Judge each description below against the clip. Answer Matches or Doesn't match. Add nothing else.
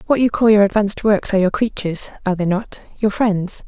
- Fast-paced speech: Matches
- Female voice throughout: Matches